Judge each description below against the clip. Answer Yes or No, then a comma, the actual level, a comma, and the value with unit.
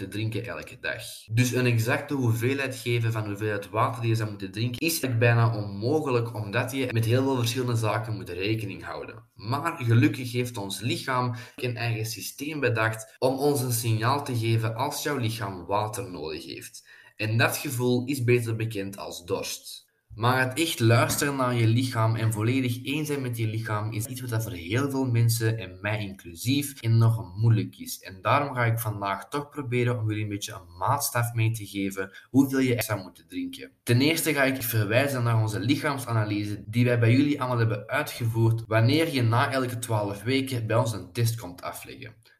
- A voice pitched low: Yes, low, 120 Hz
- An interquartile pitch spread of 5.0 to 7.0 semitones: No, average, 2.8 semitones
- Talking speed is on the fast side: No, average, 190 wpm